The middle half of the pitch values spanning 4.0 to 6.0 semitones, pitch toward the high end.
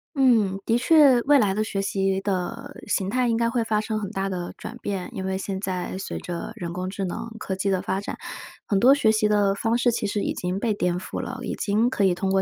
No: average, 3.2 semitones; high, 200 Hz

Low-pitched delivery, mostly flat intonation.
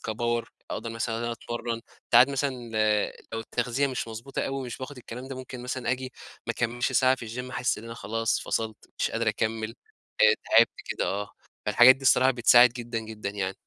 Yes: low, 120 Hz; narrow, 2.1 semitones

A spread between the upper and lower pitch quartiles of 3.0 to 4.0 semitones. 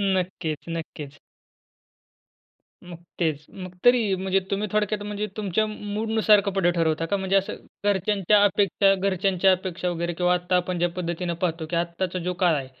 No: narrow, 2.6 semitones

